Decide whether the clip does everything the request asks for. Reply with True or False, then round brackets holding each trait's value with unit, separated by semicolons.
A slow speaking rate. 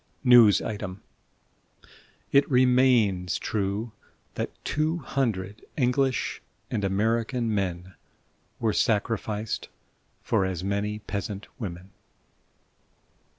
True (85 wpm)